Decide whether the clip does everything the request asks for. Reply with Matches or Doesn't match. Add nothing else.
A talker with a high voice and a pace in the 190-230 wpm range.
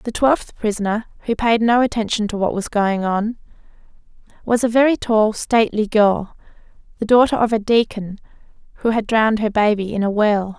Doesn't match